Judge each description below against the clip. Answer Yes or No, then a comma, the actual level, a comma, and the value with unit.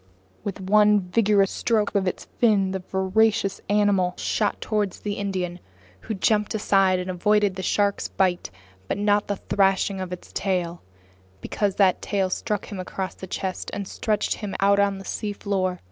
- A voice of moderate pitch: No, high, 195 Hz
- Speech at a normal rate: Yes, average, 165 wpm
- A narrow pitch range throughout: Yes, narrow, 1.7 semitones